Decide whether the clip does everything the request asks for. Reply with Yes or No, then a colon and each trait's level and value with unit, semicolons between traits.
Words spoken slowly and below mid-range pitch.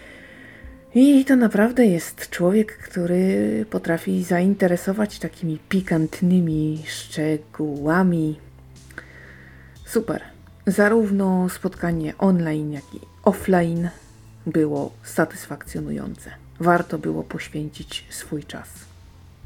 No: slow, 75 wpm; medium, 165 Hz